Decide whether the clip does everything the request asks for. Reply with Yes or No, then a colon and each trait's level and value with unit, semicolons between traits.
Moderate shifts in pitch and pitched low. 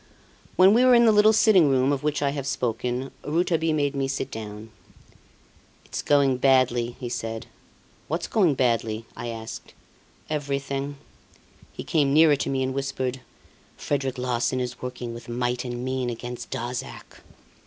Yes: average, 3.0 semitones; low, 130 Hz